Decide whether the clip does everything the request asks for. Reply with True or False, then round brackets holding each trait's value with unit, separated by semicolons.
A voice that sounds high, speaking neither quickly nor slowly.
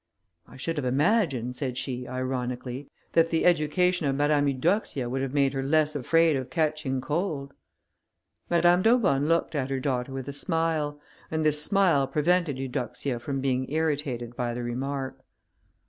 False (140 Hz; 160 wpm)